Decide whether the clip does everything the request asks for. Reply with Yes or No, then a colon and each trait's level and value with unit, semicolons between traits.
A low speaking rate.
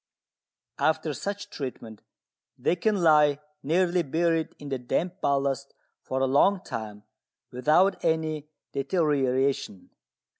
Yes: slow, 110 wpm